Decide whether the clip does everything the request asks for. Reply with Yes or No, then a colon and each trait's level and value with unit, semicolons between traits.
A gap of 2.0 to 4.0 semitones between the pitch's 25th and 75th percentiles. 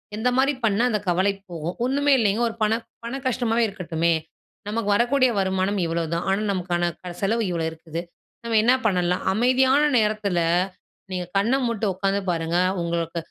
No: average, 5.0 semitones